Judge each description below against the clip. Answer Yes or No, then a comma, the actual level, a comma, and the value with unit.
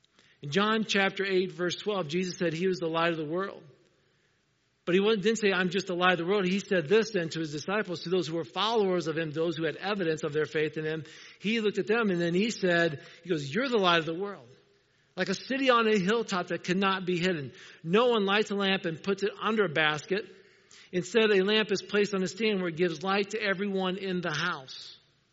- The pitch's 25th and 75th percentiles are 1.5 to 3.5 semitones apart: Yes, average, 3.1 semitones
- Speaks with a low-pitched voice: No, medium, 185 Hz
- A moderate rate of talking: No, fast, 240 wpm